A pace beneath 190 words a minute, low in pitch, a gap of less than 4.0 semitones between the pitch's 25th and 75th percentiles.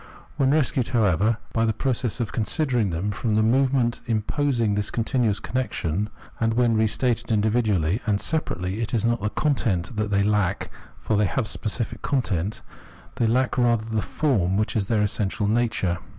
Yes: average, 170 wpm; low, 110 Hz; average, 2.9 semitones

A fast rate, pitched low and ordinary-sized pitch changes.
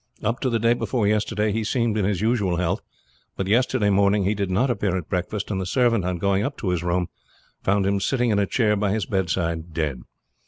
Yes: fast, 230 wpm; low, 100 Hz; average, 3.3 semitones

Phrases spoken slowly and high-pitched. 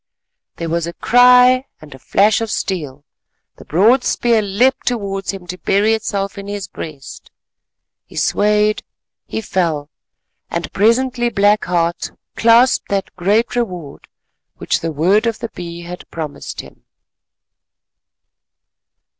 Yes: slow, 130 wpm; high, 200 Hz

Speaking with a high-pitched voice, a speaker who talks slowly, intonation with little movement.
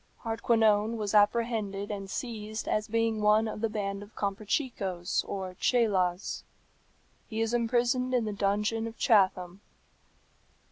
Yes: high, 215 Hz; slow, 130 wpm; narrow, 2.3 semitones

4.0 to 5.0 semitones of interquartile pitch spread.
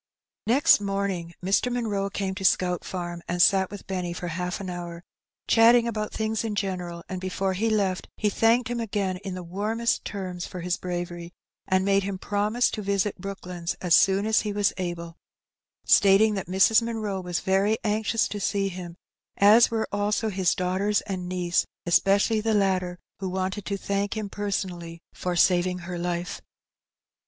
No: narrow, 2.5 semitones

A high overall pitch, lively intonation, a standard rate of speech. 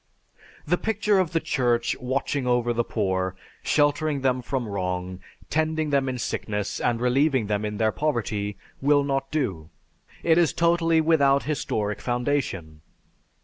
No: low, 130 Hz; wide, 6.1 semitones; average, 145 wpm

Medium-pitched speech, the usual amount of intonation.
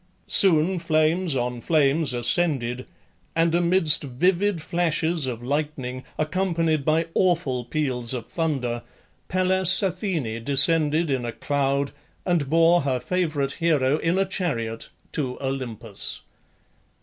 Yes: medium, 155 Hz; average, 4.8 semitones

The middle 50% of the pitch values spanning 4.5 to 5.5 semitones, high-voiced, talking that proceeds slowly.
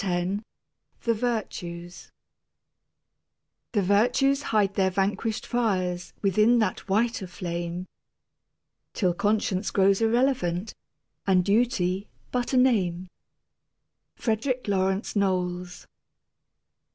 No: average, 3.8 semitones; high, 200 Hz; slow, 90 wpm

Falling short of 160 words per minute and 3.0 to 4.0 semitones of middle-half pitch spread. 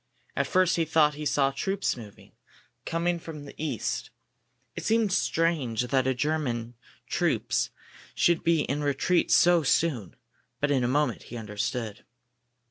No: average, 140 wpm; average, 5.1 semitones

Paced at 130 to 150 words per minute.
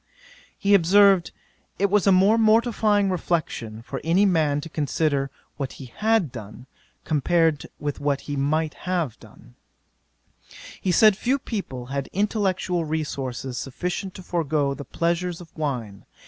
Yes: average, 140 wpm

